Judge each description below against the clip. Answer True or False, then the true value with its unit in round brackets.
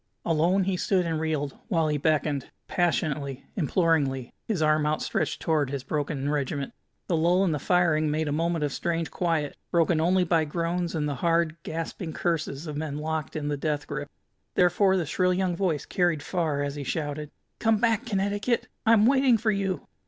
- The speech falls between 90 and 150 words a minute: False (180 wpm)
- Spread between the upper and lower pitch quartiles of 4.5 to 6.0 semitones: False (3.3 semitones)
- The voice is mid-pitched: True (160 Hz)